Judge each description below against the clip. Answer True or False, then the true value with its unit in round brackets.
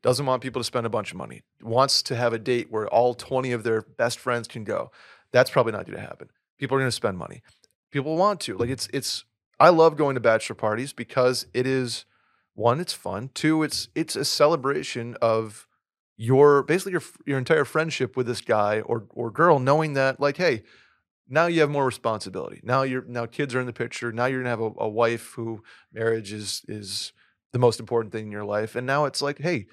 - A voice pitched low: True (125 Hz)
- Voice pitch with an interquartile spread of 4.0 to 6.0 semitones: False (3.3 semitones)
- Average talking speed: False (220 wpm)